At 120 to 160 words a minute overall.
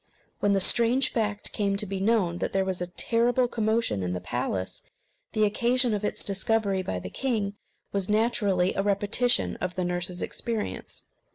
No: average, 170 wpm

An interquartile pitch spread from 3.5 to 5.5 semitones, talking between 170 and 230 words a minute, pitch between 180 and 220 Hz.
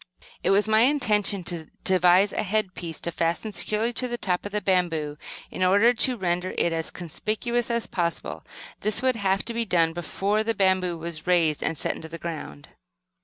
Yes: average, 4.1 semitones; average, 190 wpm; high, 190 Hz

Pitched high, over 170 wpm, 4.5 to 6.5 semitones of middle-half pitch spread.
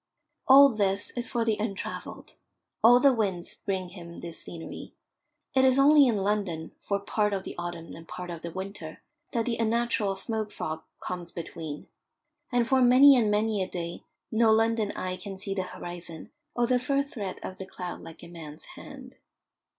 Yes: high, 200 Hz; average, 180 wpm; average, 4.9 semitones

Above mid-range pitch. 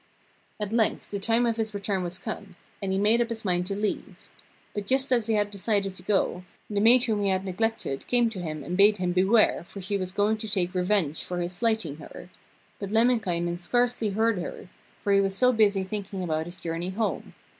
Yes: high, 200 Hz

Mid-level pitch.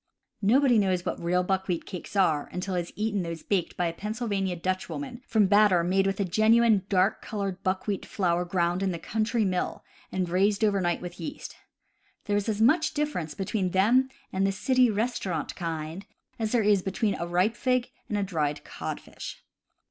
No: high, 195 Hz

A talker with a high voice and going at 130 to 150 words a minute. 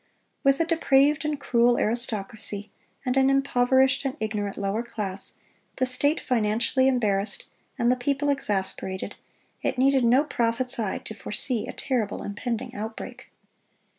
Yes: high, 245 Hz; slow, 135 wpm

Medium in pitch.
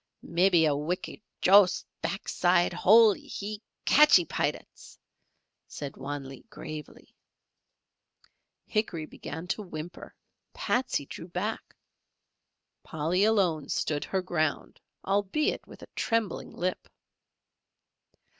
Yes: medium, 180 Hz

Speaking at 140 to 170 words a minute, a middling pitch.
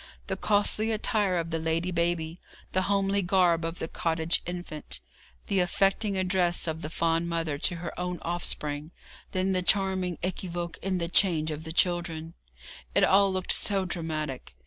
Yes: average, 165 wpm; medium, 175 Hz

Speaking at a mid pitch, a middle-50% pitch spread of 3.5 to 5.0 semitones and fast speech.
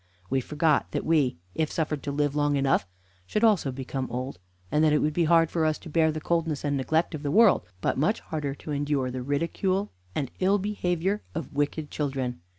No: medium, 150 Hz; average, 3.0 semitones; fast, 210 wpm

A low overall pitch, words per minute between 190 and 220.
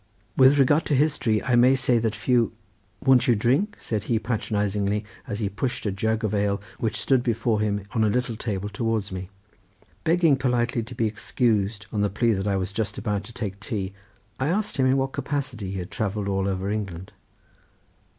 Yes: low, 110 Hz; average, 200 wpm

